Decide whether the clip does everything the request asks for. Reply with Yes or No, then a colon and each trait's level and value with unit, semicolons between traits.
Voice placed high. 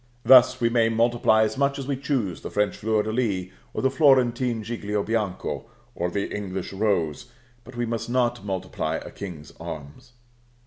No: low, 110 Hz